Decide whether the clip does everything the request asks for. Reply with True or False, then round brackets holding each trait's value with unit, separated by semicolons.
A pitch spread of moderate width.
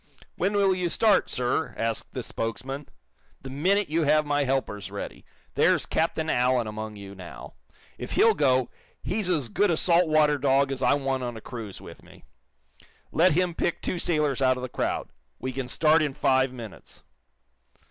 True (4.6 semitones)